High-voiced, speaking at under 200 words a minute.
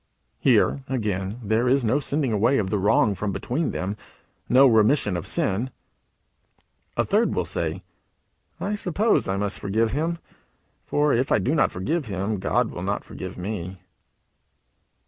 No: low, 110 Hz; average, 160 wpm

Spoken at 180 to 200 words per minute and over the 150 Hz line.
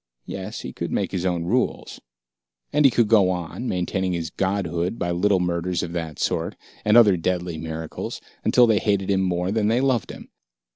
No: average, 190 wpm; very low, 90 Hz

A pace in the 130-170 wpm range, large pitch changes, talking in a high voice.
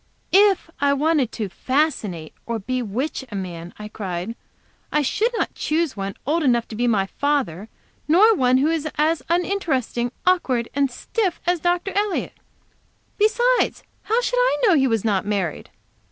Yes: average, 160 wpm; wide, 7.7 semitones; very high, 270 Hz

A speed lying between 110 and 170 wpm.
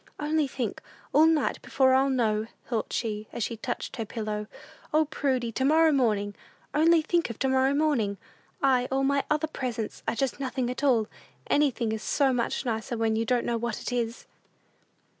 No: average, 185 wpm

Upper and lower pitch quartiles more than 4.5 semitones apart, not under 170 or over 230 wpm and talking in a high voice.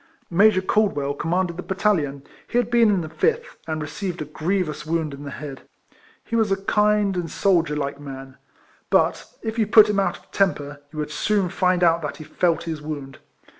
No: average, 5.1 semitones; average, 200 wpm; medium, 170 Hz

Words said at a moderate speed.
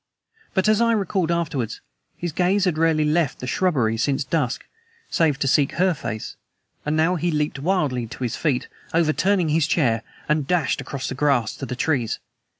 Yes: average, 180 wpm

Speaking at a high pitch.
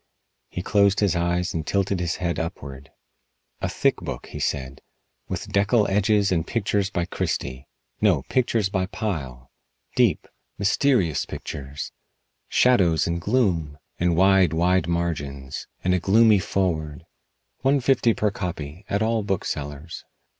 No: very low, 90 Hz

